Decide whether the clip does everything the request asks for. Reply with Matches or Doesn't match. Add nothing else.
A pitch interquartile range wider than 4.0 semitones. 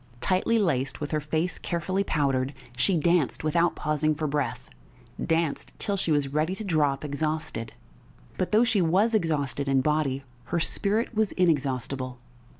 Matches